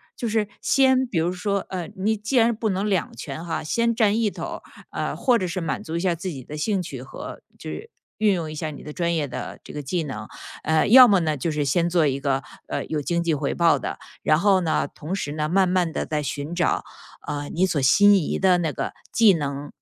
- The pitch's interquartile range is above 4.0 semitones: Yes, average, 4.8 semitones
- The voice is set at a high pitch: No, medium, 170 Hz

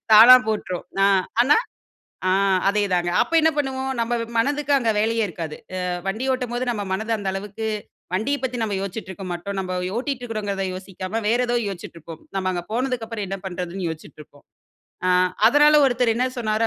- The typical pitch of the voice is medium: No, high, 215 Hz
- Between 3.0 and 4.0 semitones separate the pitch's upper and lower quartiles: No, average, 4.6 semitones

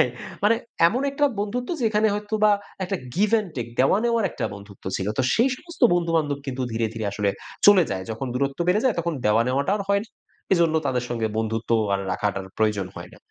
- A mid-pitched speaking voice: Yes, medium, 145 Hz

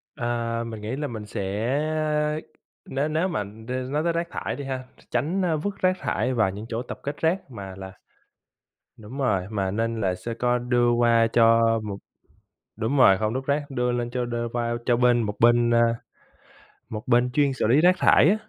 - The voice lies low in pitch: Yes, low, 120 Hz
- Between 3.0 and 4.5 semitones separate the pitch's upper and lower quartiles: Yes, average, 3.3 semitones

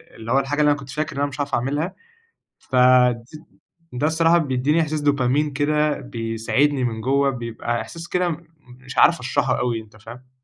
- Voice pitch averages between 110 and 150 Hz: Yes, medium, 140 Hz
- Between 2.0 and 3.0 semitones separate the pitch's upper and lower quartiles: No, average, 3.4 semitones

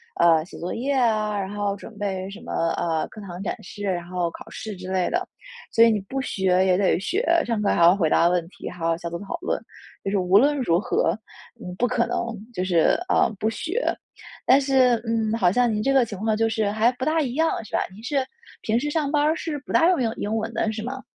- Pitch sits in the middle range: No, high, 215 Hz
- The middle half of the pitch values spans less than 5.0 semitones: No, wide, 5.4 semitones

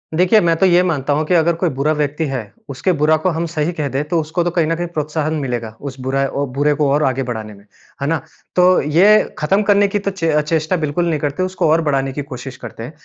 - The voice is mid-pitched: Yes, medium, 155 Hz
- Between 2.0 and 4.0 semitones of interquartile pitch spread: Yes, average, 3.7 semitones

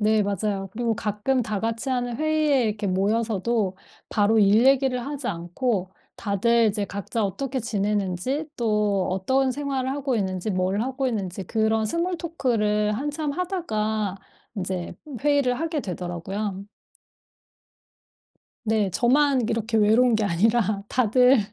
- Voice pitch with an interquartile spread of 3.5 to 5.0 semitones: Yes, average, 4.4 semitones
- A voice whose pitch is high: Yes, high, 220 Hz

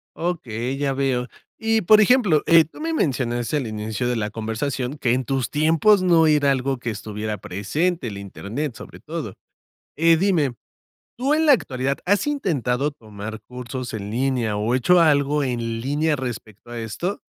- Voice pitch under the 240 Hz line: Yes, low, 135 Hz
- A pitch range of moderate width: No, wide, 5.9 semitones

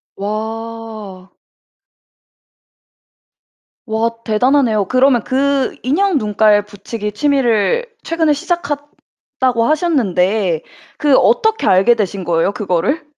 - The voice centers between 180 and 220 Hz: No, high, 230 Hz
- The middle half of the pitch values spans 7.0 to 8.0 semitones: No, wide, 5.5 semitones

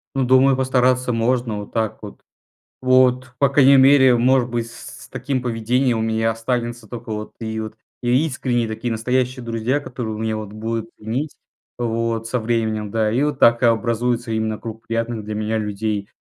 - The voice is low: Yes, low, 115 Hz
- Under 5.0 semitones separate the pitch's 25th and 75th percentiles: Yes, narrow, 2.4 semitones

